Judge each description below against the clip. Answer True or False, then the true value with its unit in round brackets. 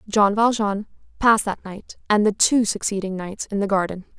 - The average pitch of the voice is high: True (205 Hz)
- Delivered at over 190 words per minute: False (185 wpm)